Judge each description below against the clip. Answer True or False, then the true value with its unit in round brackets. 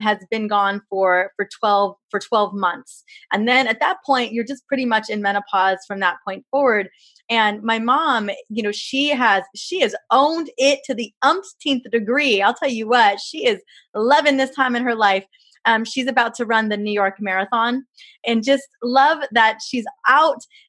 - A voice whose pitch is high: True (235 Hz)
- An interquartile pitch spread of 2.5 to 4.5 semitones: False (4.9 semitones)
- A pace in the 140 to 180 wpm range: False (190 wpm)